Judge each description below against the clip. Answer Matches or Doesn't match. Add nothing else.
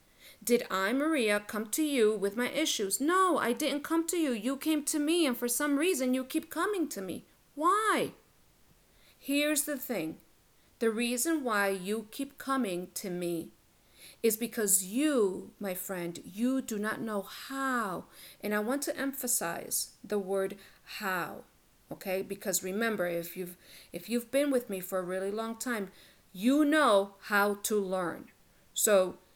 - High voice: Matches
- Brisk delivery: Doesn't match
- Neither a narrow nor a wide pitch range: Doesn't match